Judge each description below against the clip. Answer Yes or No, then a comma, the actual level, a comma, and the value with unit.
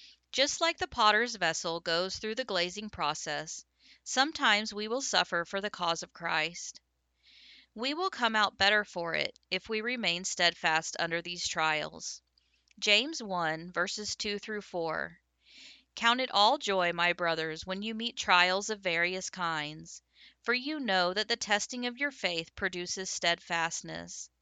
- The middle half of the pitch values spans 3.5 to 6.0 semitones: Yes, average, 4.4 semitones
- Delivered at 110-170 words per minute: Yes, average, 155 wpm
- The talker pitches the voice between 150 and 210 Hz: Yes, medium, 185 Hz